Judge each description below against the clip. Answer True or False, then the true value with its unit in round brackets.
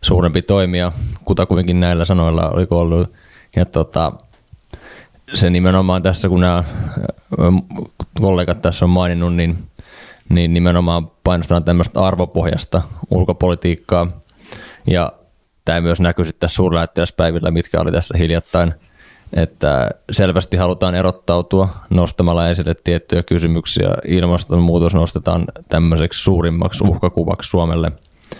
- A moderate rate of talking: True (110 wpm)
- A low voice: True (85 Hz)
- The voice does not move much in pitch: True (1.3 semitones)